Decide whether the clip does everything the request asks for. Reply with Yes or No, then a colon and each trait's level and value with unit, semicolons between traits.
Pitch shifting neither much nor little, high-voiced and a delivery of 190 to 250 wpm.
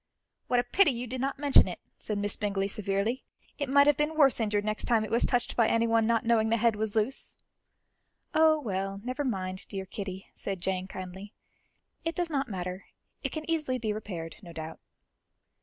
Yes: average, 5.0 semitones; high, 220 Hz; average, 195 wpm